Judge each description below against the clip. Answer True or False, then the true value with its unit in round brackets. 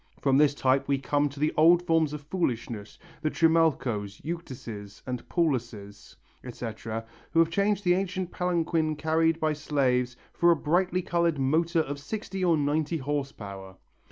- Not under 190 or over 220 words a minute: False (155 wpm)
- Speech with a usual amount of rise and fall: True (4.7 semitones)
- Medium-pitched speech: True (150 Hz)